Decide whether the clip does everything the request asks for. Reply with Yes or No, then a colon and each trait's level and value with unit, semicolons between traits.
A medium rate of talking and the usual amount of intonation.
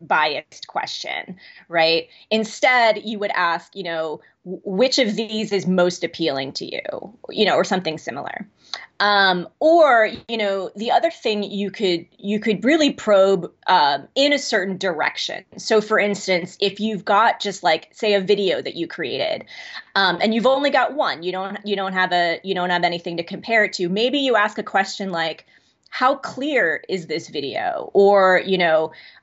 Yes: average, 180 wpm; average, 3.5 semitones